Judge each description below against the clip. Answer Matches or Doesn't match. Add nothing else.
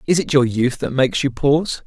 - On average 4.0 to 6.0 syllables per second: Matches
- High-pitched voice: Doesn't match